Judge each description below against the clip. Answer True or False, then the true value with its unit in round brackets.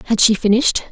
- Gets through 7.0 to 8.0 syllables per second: True (7.6 syllables/s)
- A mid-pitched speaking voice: False (220 Hz)